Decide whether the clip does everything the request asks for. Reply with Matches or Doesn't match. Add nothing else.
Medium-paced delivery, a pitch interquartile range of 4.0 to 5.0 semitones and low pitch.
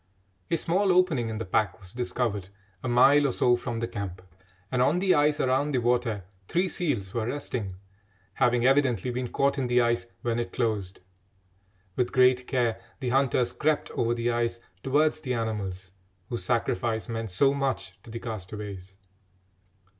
Doesn't match